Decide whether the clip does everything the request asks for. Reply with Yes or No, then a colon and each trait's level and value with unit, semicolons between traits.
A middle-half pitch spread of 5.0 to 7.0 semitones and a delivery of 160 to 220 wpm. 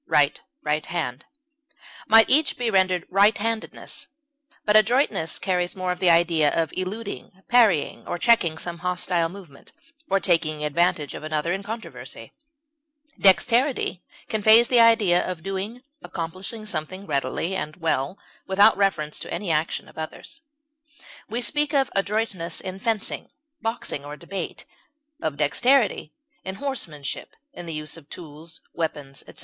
No: wide, 5.4 semitones; average, 145 wpm